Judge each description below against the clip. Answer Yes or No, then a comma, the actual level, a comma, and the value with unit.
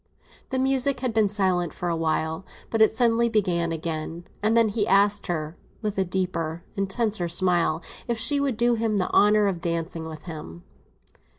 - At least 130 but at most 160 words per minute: No, average, 180 wpm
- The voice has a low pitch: No, high, 195 Hz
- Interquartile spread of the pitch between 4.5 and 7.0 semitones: Yes, average, 4.9 semitones